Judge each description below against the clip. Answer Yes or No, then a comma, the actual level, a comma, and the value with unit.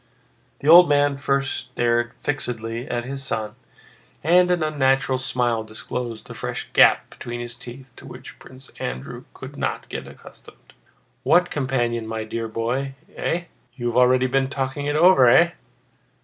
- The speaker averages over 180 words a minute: No, average, 155 wpm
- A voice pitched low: Yes, low, 130 Hz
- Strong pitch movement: No, average, 2.9 semitones